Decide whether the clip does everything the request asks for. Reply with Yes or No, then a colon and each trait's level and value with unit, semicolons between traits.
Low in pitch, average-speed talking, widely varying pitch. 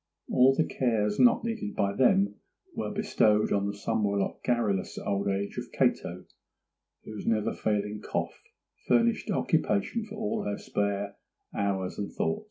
No: low, 105 Hz; average, 145 wpm; average, 4.0 semitones